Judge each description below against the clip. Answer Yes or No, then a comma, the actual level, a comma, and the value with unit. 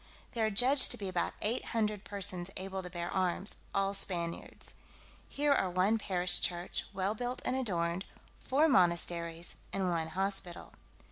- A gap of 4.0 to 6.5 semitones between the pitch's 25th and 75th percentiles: No, average, 3.3 semitones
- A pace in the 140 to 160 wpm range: Yes, average, 155 wpm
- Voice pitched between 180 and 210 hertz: Yes, high, 190 Hz